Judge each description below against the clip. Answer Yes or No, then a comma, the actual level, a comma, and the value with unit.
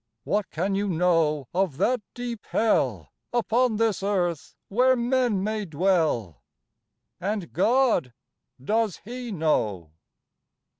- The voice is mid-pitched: No, high, 200 Hz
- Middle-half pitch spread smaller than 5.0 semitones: No, wide, 5.6 semitones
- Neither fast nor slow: No, slow, 110 wpm